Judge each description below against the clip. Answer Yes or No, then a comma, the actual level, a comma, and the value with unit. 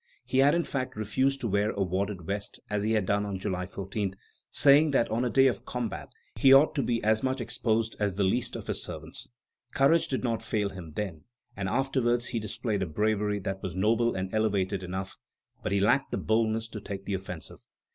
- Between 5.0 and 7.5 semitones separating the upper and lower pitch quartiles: No, average, 3.8 semitones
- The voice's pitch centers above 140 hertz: No, low, 105 Hz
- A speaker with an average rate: No, fast, 210 wpm